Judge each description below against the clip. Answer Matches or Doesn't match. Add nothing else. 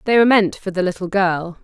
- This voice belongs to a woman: Matches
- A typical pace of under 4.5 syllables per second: Doesn't match